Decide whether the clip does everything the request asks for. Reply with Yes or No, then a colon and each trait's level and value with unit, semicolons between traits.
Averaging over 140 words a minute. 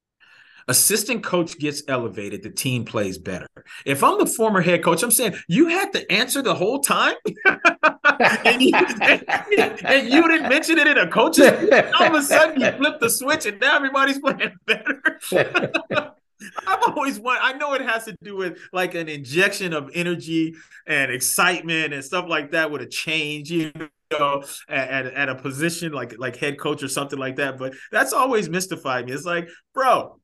Yes: average, 185 wpm